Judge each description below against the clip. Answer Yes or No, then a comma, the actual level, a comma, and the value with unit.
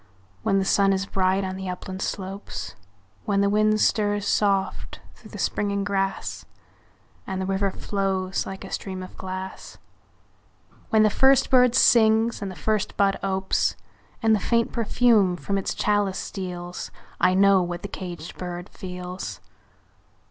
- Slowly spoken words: No, average, 155 wpm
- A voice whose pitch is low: No, high, 195 Hz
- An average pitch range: No, narrow, 1.7 semitones